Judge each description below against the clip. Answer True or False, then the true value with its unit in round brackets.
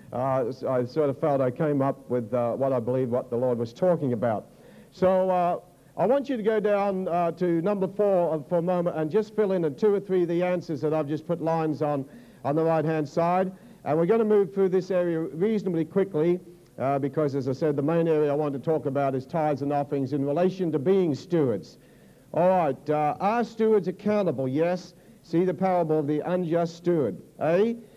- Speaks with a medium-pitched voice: True (165 Hz)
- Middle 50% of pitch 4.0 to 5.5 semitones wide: True (4.3 semitones)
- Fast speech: True (220 wpm)